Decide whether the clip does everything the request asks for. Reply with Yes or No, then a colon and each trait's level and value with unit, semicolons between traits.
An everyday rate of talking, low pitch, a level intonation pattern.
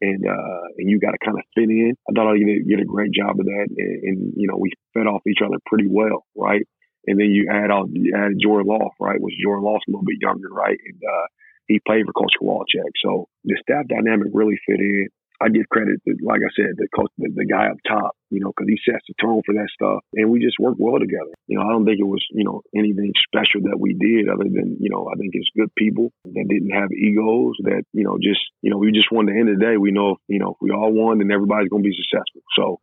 No: fast, 270 wpm; low, 105 Hz; narrow, 1.3 semitones